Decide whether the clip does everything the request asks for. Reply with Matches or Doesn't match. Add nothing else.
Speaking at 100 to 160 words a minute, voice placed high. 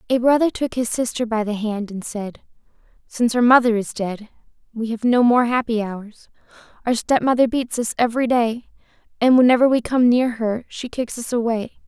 Doesn't match